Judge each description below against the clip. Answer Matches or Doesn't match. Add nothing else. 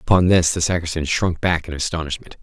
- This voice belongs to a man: Matches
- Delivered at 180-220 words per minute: Matches